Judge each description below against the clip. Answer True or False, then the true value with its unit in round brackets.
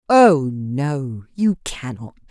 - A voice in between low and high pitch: True (150 Hz)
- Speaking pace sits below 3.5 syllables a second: True (2.8 syllables/s)